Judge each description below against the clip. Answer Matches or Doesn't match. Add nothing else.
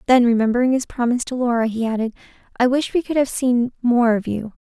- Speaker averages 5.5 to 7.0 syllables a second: Matches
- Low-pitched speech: Doesn't match